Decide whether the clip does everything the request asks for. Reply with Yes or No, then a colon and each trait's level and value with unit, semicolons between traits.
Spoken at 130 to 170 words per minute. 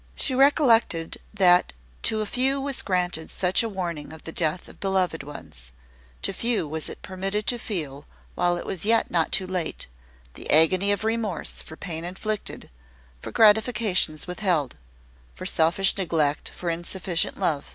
Yes: average, 155 wpm